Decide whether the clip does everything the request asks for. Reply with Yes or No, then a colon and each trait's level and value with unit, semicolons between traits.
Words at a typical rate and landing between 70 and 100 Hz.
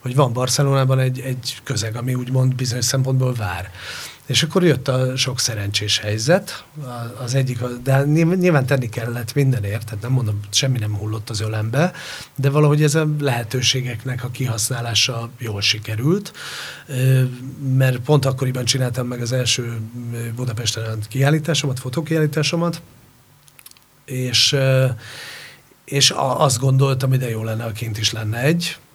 No: average, 135 wpm; low, 130 Hz